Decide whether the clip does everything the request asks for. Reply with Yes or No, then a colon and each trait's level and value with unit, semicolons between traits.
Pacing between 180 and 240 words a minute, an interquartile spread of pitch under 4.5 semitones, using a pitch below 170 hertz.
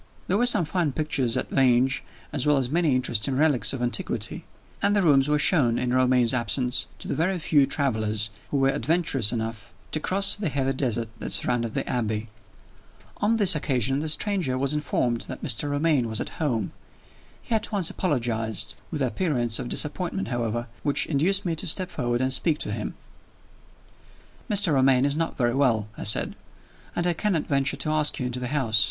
No: average, 190 wpm; average, 4.8 semitones; low, 135 Hz